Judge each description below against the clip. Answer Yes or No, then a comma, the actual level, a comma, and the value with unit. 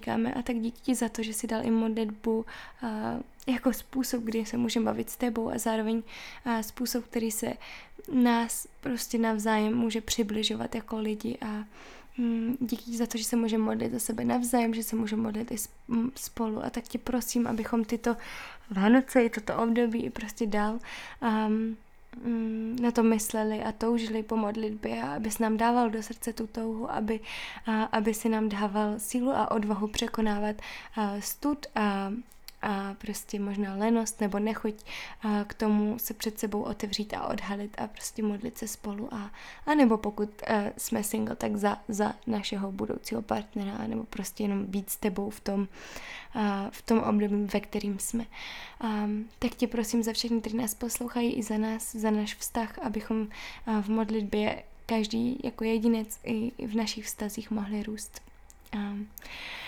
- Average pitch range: No, narrow, 1.6 semitones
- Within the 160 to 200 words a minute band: Yes, average, 170 wpm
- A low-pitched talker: No, high, 225 Hz